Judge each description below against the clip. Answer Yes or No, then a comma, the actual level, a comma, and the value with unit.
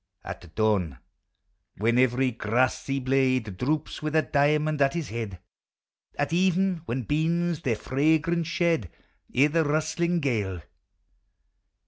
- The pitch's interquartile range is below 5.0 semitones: No, average, 5.3 semitones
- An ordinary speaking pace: No, slow, 120 wpm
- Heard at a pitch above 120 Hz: Yes, medium, 140 Hz